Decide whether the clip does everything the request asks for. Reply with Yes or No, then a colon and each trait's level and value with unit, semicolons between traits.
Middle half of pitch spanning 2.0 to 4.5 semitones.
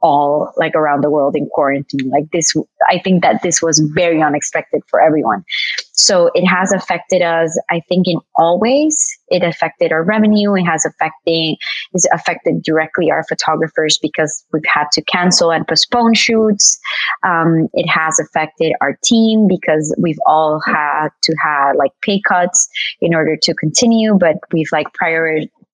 Yes: average, 2.9 semitones